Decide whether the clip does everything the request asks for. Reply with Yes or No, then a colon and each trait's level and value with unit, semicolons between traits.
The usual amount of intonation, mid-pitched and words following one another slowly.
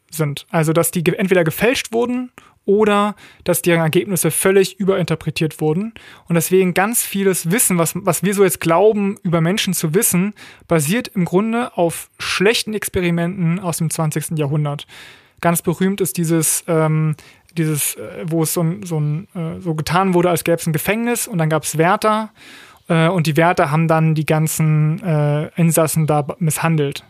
No: average, 3.2 semitones; medium, 170 Hz; average, 170 wpm